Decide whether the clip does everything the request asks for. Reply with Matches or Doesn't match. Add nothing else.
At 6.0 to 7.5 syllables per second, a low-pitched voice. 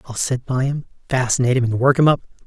Matches